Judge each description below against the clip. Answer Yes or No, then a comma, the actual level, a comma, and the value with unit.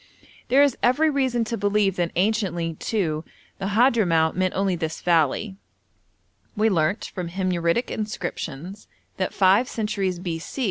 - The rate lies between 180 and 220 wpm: No, slow, 135 wpm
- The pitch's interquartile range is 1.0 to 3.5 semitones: No, average, 4.3 semitones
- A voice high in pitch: Yes, high, 195 Hz